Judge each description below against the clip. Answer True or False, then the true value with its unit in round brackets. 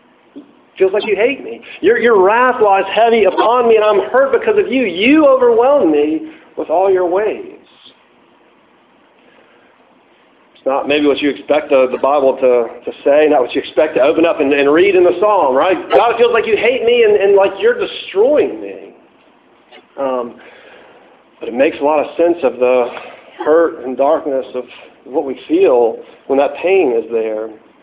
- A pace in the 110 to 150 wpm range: False (185 wpm)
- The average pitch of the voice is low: False (200 Hz)